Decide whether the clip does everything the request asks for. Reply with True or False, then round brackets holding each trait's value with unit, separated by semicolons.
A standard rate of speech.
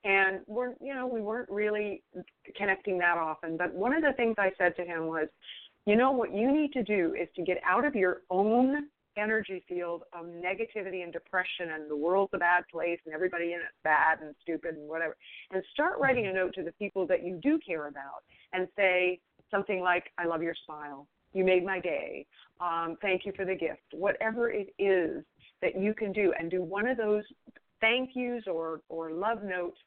False (210 wpm)